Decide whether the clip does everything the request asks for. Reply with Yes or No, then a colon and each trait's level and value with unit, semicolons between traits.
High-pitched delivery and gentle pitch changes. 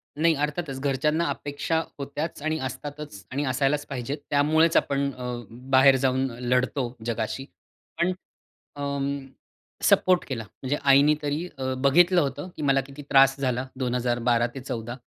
No: medium, 140 Hz; narrow, 2.3 semitones